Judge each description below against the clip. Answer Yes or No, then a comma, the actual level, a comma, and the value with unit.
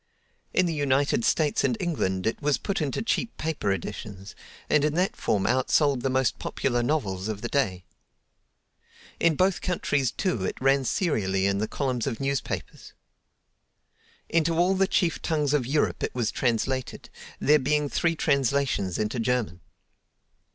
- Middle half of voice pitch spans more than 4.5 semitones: Yes, wide, 5.5 semitones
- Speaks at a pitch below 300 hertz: Yes, low, 135 Hz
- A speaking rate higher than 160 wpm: No, average, 155 wpm